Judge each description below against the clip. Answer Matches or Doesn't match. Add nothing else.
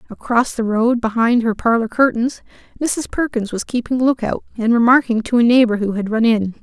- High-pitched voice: Matches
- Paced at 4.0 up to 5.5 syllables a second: Matches